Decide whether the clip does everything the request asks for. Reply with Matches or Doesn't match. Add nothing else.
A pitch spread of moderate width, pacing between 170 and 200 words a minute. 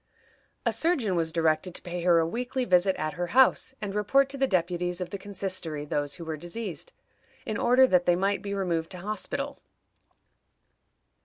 Matches